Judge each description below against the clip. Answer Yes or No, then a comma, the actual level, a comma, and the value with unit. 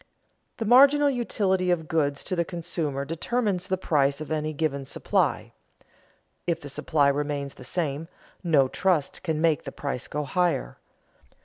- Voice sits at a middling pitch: Yes, medium, 160 Hz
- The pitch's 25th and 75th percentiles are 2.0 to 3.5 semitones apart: No, average, 4.2 semitones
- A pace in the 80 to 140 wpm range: No, average, 150 wpm